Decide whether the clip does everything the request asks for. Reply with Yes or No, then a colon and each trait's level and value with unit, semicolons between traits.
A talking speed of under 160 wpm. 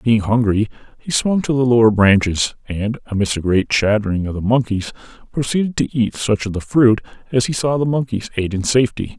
No: fast, 205 wpm